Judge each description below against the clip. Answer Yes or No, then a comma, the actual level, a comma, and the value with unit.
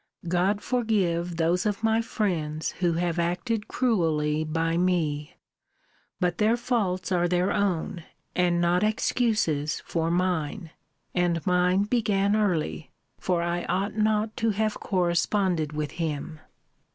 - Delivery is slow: Yes, slow, 125 wpm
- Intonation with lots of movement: No, average, 3.8 semitones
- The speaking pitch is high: No, medium, 180 Hz